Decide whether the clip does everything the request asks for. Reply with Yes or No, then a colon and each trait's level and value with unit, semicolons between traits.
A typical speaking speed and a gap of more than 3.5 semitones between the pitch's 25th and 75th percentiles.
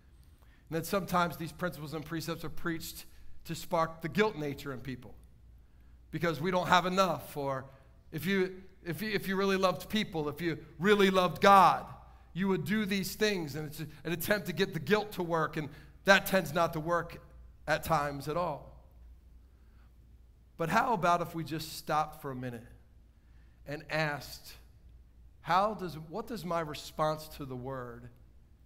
Yes: average, 175 wpm; average, 5.1 semitones